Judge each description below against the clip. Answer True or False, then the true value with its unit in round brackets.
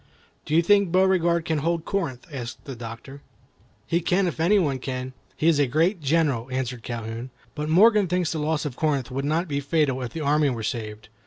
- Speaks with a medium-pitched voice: True (150 Hz)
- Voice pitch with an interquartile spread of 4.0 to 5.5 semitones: True (4.7 semitones)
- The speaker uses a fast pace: True (210 wpm)